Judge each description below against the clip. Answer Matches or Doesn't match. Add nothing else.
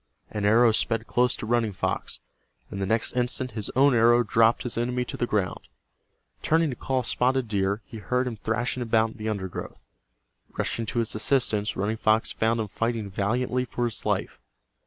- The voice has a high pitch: Doesn't match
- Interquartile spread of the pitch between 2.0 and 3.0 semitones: Matches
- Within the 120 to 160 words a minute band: Doesn't match